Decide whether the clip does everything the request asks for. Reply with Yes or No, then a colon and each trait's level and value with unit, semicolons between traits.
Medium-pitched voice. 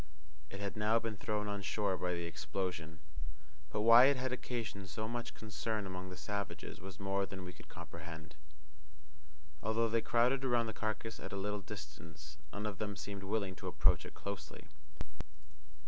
No: low, 100 Hz